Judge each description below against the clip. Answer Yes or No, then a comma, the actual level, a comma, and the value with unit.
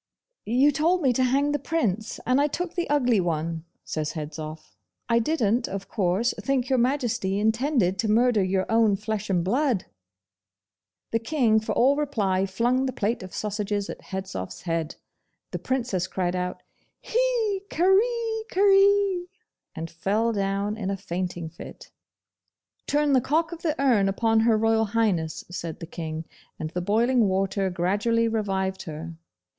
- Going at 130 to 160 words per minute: Yes, average, 155 wpm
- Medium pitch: No, high, 220 Hz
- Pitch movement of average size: No, wide, 6.1 semitones